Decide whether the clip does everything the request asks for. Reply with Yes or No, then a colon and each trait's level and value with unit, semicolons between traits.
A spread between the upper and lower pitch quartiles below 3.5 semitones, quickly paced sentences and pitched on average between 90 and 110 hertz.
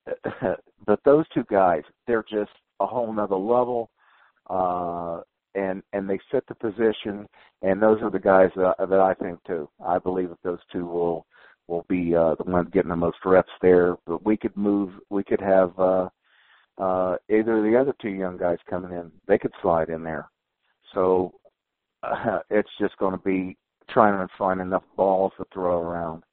No: average, 2.7 semitones; average, 185 wpm; very low, 95 Hz